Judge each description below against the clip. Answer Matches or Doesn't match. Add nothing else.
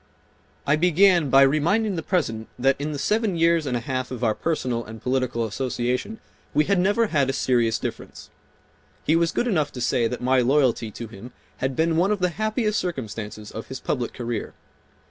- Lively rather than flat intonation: Matches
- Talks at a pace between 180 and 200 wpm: Matches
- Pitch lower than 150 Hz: Matches